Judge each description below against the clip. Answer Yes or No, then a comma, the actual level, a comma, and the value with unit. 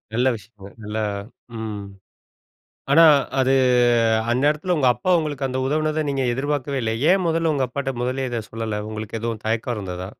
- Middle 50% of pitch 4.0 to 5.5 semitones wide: Yes, average, 4.7 semitones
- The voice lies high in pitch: No, low, 130 Hz